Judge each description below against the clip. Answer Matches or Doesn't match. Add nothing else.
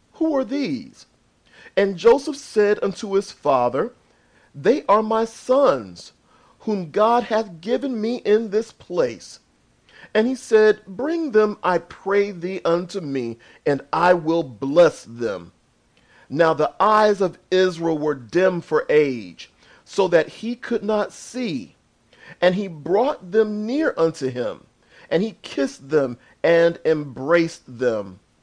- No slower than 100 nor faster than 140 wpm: Matches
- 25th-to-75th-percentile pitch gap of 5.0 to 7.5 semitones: Matches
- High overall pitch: Matches